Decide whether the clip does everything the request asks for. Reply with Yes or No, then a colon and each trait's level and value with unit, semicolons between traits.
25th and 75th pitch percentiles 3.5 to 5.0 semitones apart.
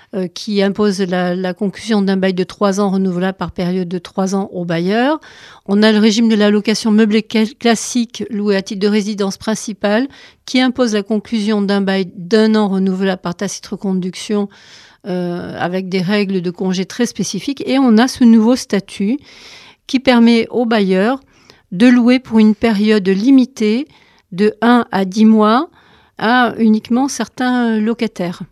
No: average, 3.1 semitones